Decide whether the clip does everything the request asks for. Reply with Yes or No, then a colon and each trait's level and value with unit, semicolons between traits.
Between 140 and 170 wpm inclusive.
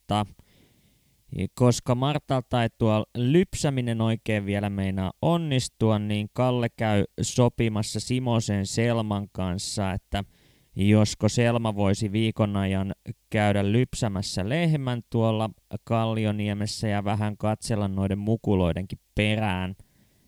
No: average, 100 wpm